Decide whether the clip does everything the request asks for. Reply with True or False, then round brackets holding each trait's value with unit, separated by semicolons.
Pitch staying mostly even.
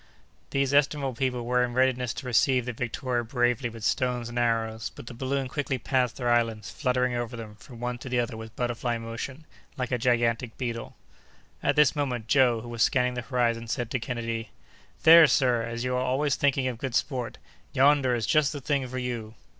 True (2.0 semitones)